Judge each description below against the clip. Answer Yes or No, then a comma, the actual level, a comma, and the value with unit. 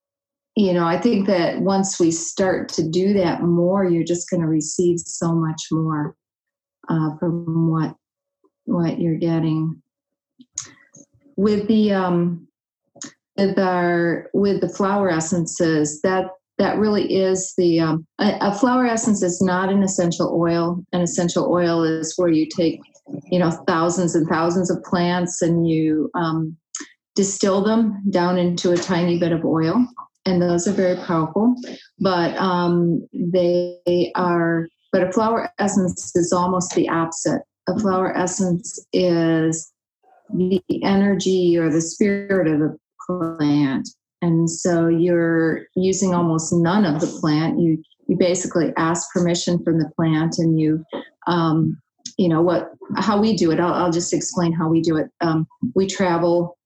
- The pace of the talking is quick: No, average, 150 wpm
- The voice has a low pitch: No, medium, 175 Hz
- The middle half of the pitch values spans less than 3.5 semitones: Yes, narrow, 2.6 semitones